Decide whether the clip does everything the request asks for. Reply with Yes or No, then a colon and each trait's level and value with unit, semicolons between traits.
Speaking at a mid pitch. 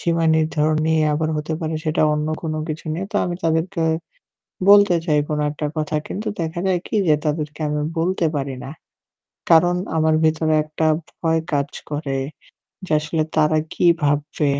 Yes: medium, 155 Hz